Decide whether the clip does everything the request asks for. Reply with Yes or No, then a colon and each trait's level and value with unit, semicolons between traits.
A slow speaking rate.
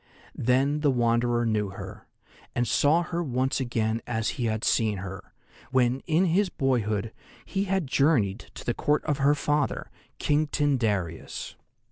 No: average, 150 wpm